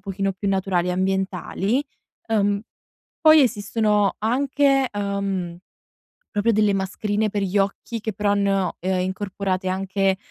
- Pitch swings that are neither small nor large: No, narrow, 1.8 semitones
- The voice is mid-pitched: No, high, 200 Hz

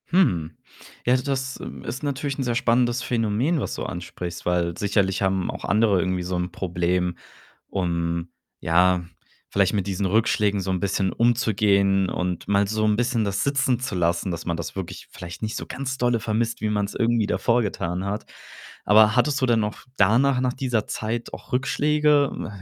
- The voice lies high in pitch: No, low, 105 Hz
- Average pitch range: Yes, average, 4.9 semitones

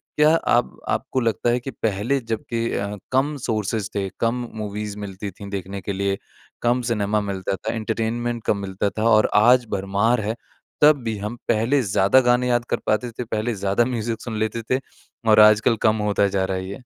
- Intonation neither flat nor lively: Yes, average, 3.0 semitones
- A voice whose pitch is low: Yes, low, 110 Hz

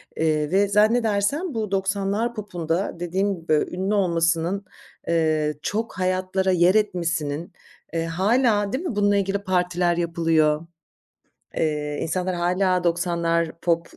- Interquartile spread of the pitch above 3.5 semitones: No, average, 3.2 semitones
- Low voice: No, medium, 180 Hz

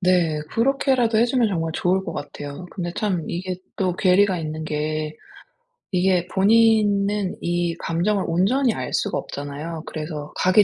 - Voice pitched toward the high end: No, medium, 180 Hz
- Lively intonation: No, average, 4.0 semitones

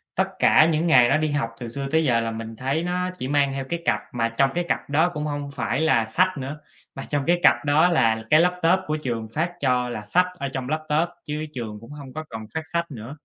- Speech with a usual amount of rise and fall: Yes, average, 4.5 semitones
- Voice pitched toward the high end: No, medium, 145 Hz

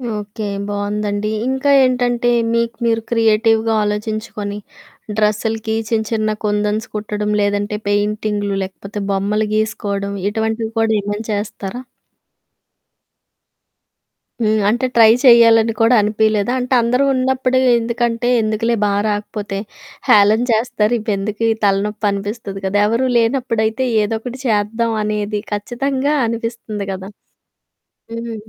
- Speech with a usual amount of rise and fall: No, narrow, 2.0 semitones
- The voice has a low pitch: No, high, 215 Hz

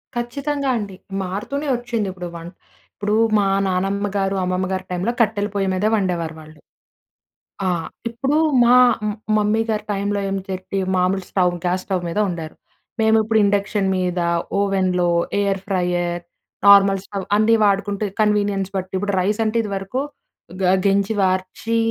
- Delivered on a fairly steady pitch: Yes, narrow, 2.2 semitones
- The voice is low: No, high, 195 Hz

